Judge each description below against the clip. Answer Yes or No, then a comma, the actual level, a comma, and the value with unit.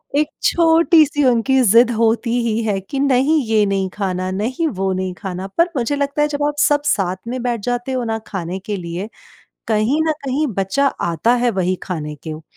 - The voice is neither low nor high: No, high, 230 Hz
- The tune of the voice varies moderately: No, wide, 6.5 semitones